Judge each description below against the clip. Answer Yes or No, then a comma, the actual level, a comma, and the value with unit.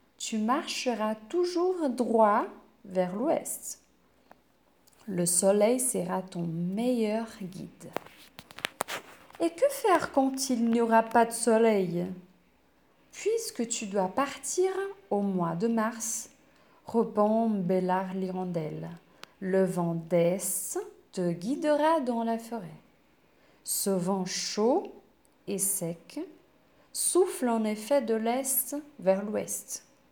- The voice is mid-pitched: No, high, 225 Hz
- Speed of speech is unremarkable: No, slow, 105 wpm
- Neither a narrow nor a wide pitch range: No, wide, 6.5 semitones